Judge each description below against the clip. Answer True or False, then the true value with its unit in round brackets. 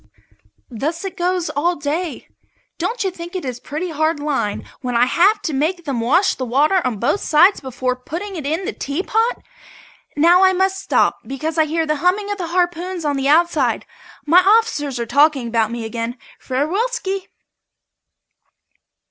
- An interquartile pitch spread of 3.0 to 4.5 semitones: False (5.3 semitones)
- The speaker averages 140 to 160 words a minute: False (170 wpm)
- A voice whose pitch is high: True (320 Hz)